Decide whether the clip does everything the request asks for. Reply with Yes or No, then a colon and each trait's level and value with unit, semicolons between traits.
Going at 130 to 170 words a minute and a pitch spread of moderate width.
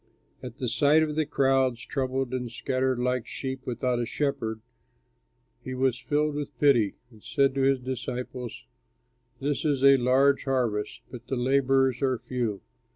No: average, 155 wpm; narrow, 1.9 semitones